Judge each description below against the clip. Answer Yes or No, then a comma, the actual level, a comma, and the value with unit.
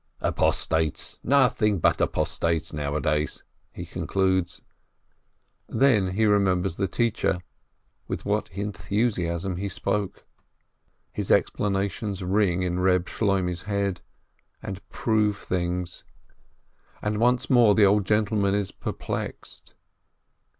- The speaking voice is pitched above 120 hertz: No, very low, 95 Hz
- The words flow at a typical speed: No, slow, 105 wpm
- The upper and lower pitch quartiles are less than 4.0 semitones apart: Yes, average, 2.9 semitones